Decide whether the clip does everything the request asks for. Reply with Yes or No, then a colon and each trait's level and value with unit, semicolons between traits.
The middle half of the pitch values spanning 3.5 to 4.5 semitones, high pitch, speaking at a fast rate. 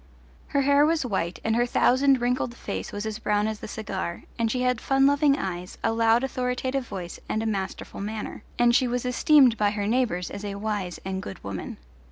Yes: average, 3.8 semitones; high, 225 Hz; fast, 210 wpm